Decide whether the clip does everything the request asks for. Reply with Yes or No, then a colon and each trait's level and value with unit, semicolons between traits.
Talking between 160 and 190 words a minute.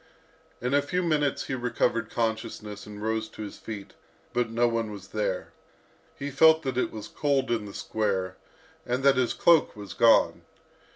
Yes: average, 175 wpm